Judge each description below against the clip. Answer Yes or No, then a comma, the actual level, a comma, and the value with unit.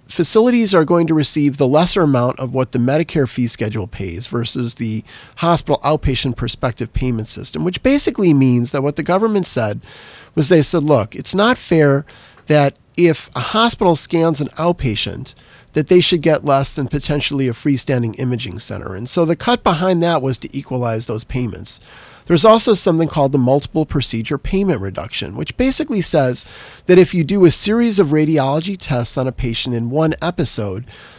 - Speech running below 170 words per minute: No, average, 180 wpm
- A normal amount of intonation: No, wide, 5.7 semitones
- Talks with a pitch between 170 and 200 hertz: No, medium, 145 Hz